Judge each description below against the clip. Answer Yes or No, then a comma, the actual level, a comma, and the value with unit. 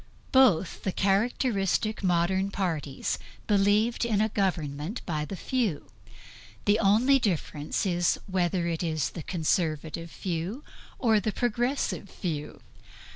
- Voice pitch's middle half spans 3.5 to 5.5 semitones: Yes, average, 4.4 semitones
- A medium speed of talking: No, slow, 115 wpm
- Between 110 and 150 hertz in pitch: No, high, 190 Hz